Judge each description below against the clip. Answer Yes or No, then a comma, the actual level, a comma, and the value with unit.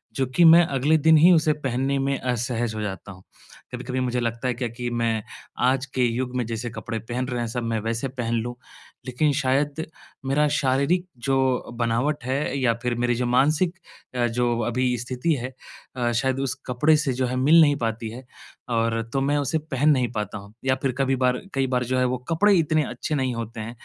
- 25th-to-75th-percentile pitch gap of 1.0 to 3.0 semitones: Yes, narrow, 2.5 semitones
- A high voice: No, low, 125 Hz